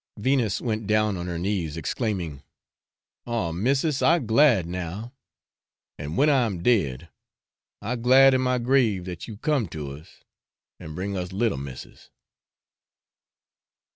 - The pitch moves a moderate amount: No, wide, 6.3 semitones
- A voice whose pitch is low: Yes, low, 105 Hz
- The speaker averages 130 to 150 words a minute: Yes, average, 140 wpm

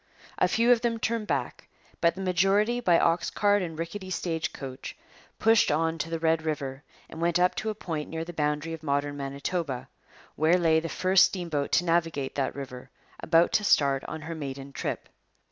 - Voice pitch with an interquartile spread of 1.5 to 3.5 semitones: No, average, 3.9 semitones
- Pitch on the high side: No, medium, 165 Hz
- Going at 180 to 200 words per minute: Yes, average, 190 wpm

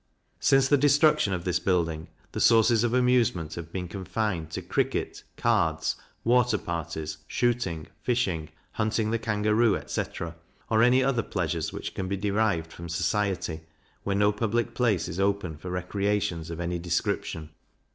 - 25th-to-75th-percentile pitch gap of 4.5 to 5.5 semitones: Yes, average, 5.2 semitones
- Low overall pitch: Yes, low, 100 Hz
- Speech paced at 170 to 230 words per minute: No, average, 150 wpm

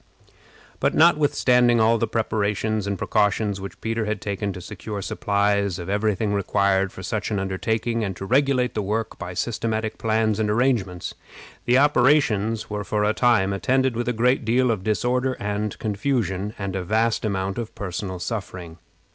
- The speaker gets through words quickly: No, average, 165 wpm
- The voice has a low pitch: Yes, low, 105 Hz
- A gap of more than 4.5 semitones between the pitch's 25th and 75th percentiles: No, average, 2.8 semitones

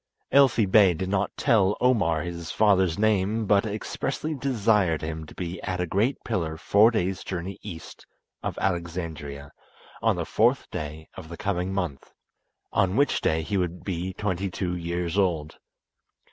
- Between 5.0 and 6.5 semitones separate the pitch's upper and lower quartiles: No, average, 3.5 semitones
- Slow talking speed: No, average, 160 wpm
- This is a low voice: Yes, very low, 95 Hz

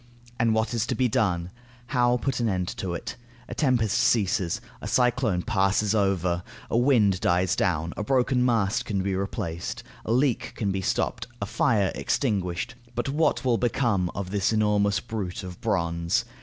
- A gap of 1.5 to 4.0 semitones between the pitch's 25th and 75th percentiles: No, average, 4.4 semitones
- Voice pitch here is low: Yes, low, 105 Hz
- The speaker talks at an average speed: Yes, average, 170 wpm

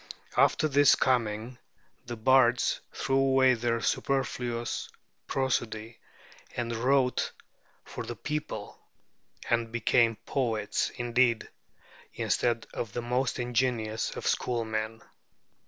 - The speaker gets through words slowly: Yes, slow, 100 wpm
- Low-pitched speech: Yes, low, 120 Hz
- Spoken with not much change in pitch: Yes, narrow, 2.2 semitones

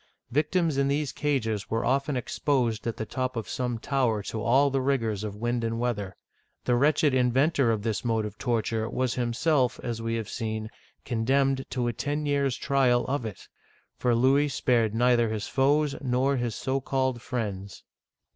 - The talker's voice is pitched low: Yes, low, 125 Hz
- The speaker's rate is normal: Yes, average, 175 wpm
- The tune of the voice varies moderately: Yes, average, 3.2 semitones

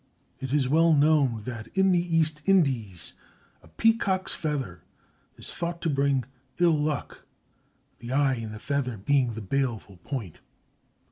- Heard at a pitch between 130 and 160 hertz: Yes, medium, 140 Hz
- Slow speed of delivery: No, average, 145 wpm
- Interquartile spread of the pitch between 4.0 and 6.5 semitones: Yes, average, 5.3 semitones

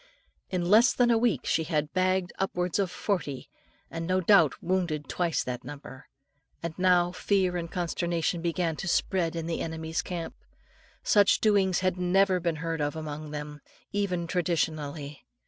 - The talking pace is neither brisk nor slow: Yes, average, 160 wpm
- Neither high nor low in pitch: Yes, medium, 175 Hz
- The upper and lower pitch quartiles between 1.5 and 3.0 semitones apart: Yes, narrow, 2.6 semitones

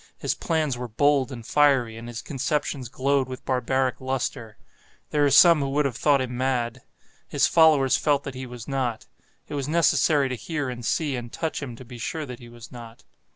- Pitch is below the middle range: Yes, low, 130 Hz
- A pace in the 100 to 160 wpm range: No, fast, 205 wpm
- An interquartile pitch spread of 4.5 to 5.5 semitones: No, average, 3.0 semitones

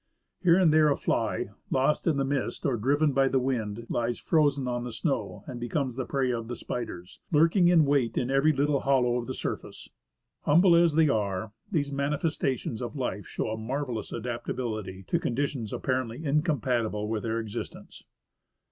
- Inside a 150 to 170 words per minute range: No, average, 180 wpm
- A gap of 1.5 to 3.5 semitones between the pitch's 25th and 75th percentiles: No, average, 4.0 semitones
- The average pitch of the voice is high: No, low, 130 Hz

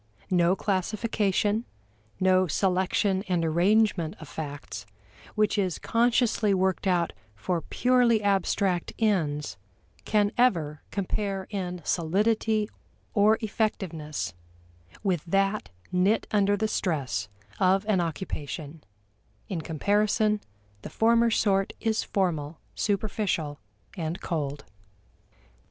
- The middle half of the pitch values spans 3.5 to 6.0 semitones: Yes, average, 4.2 semitones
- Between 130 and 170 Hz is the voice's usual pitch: No, high, 190 Hz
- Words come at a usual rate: No, slow, 100 wpm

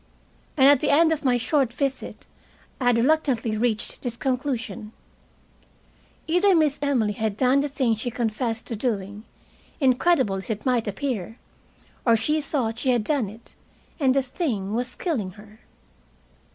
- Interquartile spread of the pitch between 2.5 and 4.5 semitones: Yes, average, 4.1 semitones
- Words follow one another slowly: No, average, 155 wpm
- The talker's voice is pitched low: No, high, 245 Hz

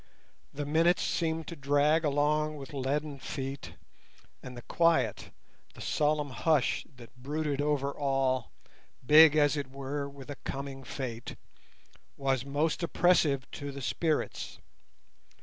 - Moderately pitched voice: Yes, medium, 145 Hz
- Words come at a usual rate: No, slow, 125 wpm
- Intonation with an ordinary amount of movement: No, narrow, 2.1 semitones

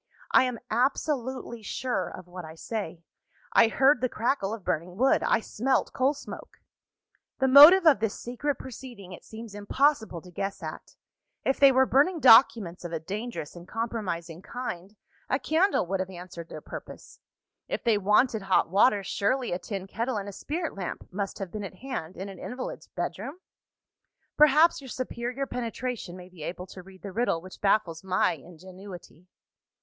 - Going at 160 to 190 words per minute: Yes, average, 175 wpm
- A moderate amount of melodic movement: No, wide, 5.9 semitones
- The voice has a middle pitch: No, high, 215 Hz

